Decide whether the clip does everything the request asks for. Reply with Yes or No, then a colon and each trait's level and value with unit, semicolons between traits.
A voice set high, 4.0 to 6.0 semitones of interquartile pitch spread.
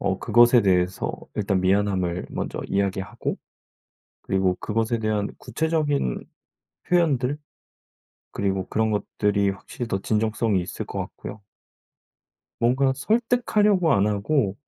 No: low, 105 Hz; average, 5.3 semitones